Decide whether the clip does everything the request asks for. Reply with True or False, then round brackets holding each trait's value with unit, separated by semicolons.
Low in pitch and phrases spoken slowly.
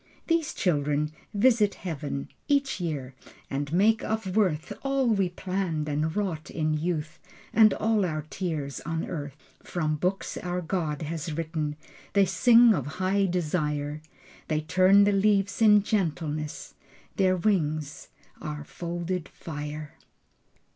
False (170 Hz; 130 wpm)